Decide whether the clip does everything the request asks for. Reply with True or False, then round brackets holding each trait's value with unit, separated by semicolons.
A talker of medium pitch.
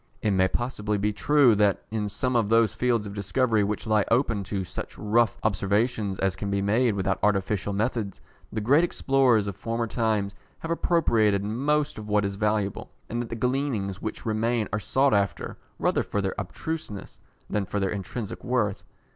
False (105 Hz)